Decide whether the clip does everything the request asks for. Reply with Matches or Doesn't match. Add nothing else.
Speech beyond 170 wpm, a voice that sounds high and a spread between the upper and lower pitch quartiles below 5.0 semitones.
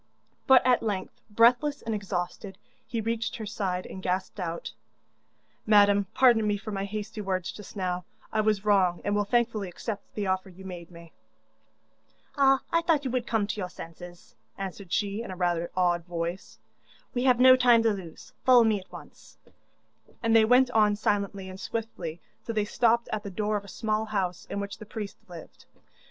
Matches